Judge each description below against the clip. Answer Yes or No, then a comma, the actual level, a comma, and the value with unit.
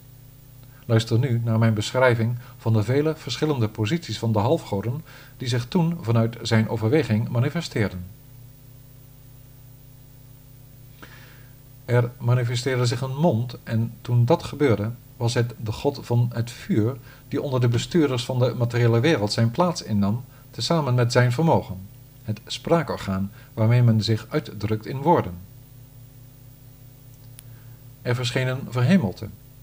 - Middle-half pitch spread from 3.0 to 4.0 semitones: No, narrow, 2.4 semitones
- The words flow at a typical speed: No, slow, 130 wpm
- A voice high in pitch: No, low, 125 Hz